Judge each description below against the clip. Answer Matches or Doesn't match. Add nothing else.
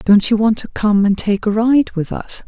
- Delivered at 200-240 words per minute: Doesn't match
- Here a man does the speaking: Doesn't match